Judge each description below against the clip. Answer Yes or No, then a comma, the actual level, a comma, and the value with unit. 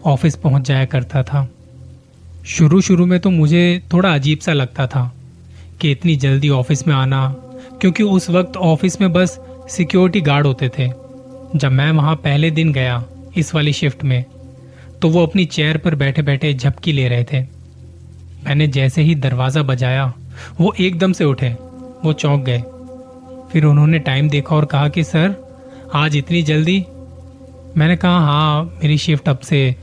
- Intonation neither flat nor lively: Yes, average, 4.1 semitones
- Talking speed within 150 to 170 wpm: Yes, average, 165 wpm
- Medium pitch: Yes, medium, 145 Hz